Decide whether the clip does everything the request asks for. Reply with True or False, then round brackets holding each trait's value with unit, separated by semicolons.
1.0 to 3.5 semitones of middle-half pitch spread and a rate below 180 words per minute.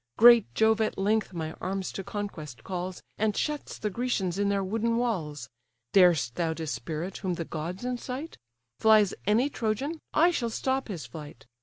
False (5.3 semitones; 165 wpm)